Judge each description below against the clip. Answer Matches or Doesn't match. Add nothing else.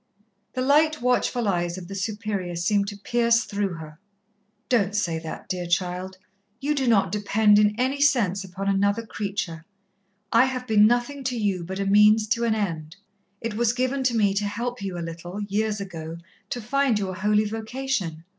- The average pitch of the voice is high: Matches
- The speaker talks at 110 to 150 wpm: Doesn't match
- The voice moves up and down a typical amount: Matches